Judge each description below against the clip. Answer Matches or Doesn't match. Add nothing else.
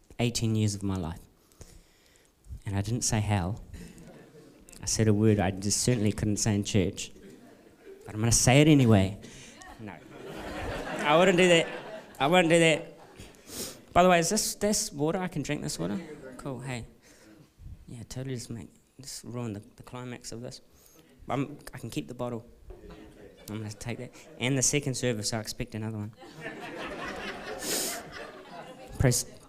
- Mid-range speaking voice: Doesn't match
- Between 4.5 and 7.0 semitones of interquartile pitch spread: Matches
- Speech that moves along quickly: Doesn't match